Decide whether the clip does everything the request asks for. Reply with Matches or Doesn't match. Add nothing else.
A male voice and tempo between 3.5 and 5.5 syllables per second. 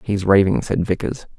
Matches